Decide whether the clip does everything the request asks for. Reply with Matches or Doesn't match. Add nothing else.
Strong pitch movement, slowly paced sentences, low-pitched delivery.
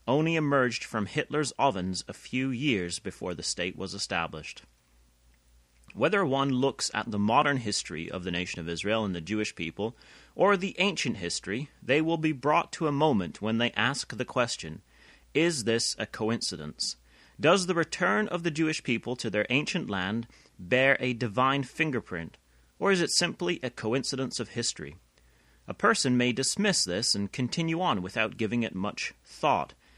Doesn't match